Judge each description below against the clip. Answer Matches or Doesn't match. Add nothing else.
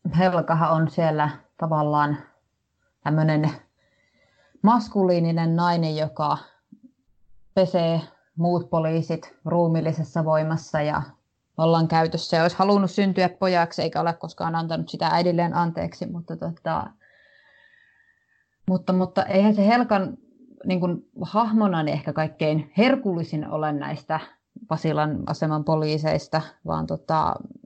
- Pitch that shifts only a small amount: Doesn't match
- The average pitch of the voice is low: Doesn't match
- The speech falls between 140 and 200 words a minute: Doesn't match